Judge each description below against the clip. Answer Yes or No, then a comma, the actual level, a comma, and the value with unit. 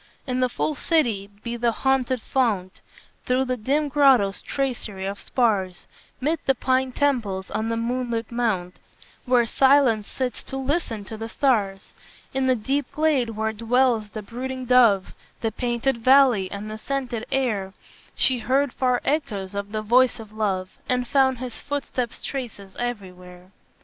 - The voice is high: Yes, high, 240 Hz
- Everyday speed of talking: Yes, average, 155 wpm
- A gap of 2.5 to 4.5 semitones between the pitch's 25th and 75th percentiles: Yes, average, 3.8 semitones